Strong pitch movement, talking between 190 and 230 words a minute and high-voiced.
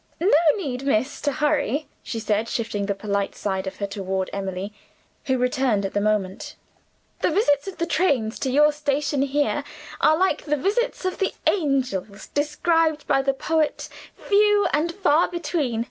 No: wide, 6.9 semitones; average, 165 wpm; very high, 275 Hz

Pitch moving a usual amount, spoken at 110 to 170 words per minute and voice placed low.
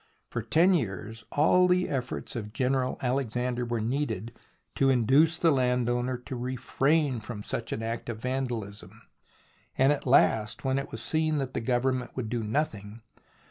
Yes: average, 3.2 semitones; average, 160 wpm; low, 125 Hz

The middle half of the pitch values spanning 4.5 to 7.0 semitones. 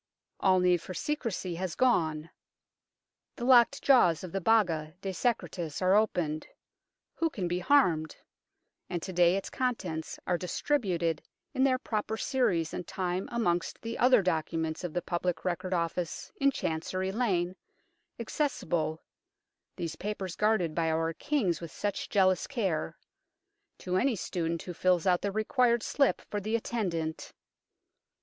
Yes: average, 4.9 semitones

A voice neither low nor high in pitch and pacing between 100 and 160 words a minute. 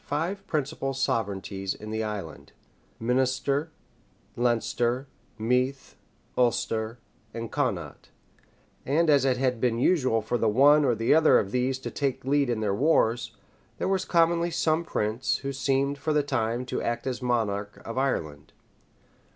No: low, 125 Hz; average, 150 wpm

